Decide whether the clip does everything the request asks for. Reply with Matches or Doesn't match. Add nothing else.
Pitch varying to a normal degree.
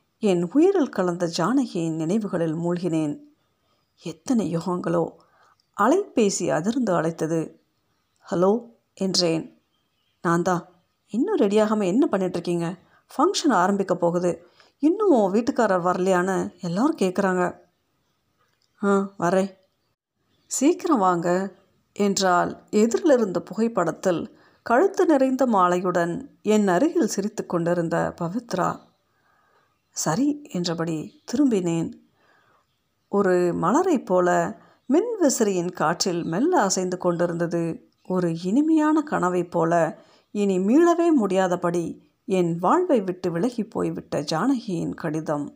Doesn't match